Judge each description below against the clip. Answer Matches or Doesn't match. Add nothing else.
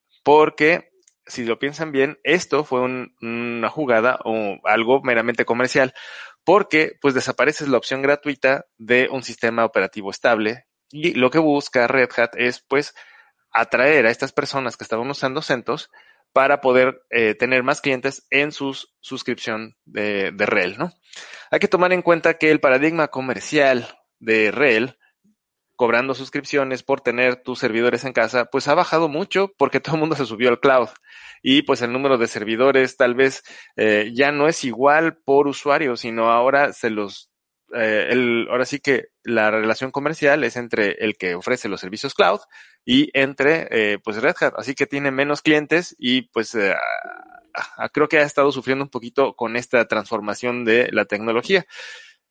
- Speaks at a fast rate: Doesn't match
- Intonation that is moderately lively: Matches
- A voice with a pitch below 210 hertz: Matches